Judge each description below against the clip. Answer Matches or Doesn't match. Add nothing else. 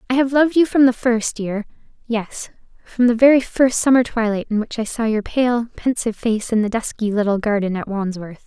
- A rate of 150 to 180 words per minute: Doesn't match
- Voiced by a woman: Matches